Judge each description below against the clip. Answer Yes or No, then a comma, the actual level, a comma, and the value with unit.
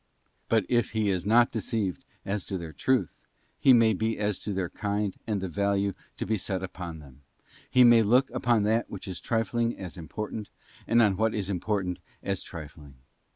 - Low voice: Yes, low, 100 Hz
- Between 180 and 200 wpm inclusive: Yes, average, 190 wpm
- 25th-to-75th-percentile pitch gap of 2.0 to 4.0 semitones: Yes, average, 3.4 semitones